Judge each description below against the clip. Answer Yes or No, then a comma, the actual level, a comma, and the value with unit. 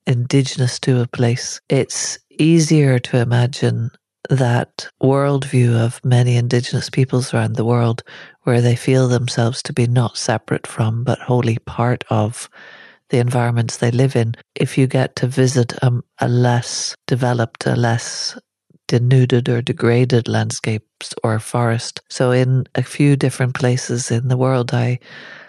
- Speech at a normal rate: Yes, average, 145 wpm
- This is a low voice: Yes, low, 125 Hz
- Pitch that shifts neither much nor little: No, narrow, 1.5 semitones